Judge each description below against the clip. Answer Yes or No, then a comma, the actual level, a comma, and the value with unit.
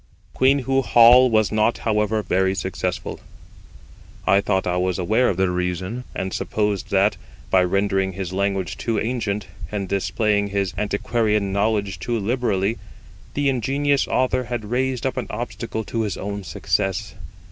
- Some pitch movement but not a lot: Yes, average, 3.7 semitones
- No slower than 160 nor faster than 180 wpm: No, average, 145 wpm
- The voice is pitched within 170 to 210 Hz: No, low, 105 Hz